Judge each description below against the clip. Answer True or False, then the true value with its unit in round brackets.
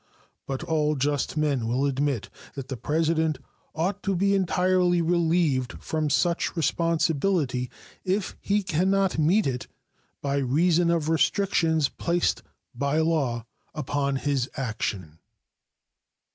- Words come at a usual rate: False (120 wpm)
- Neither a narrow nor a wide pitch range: True (4.2 semitones)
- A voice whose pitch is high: False (155 Hz)